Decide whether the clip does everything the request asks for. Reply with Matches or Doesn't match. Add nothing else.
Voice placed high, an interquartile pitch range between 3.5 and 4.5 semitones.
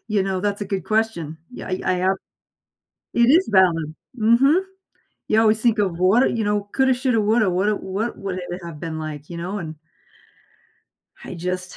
Matches